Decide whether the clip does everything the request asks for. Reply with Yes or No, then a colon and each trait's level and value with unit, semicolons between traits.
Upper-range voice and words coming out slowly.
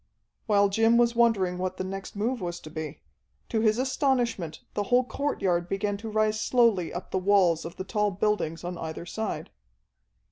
No: high, 205 Hz; average, 180 wpm